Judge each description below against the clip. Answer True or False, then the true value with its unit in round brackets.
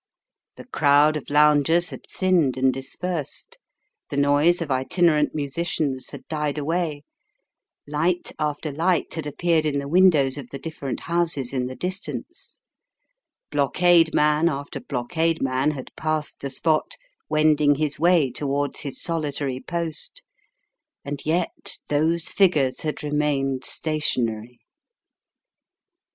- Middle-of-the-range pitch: True (150 Hz)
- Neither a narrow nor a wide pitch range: True (3.0 semitones)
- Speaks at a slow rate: True (125 wpm)